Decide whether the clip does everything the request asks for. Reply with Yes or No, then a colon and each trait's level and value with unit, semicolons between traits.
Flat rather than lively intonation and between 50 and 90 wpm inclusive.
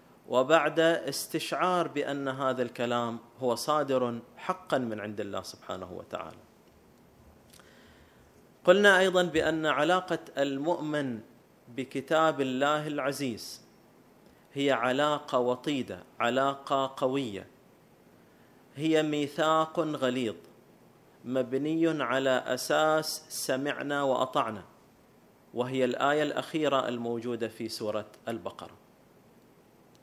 No: average, 4.3 semitones; average, 80 wpm